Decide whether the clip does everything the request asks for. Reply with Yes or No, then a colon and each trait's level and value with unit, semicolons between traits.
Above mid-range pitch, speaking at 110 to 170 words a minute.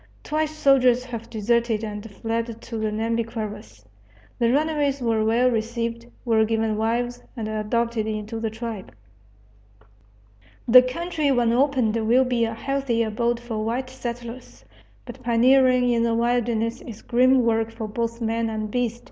Yes: high, 230 Hz; average, 150 wpm